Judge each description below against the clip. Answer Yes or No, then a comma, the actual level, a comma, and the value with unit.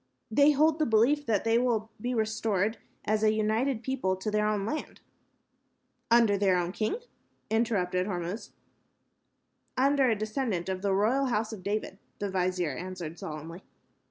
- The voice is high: Yes, high, 215 Hz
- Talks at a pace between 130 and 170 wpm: Yes, average, 155 wpm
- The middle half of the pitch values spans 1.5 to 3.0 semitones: No, average, 3.9 semitones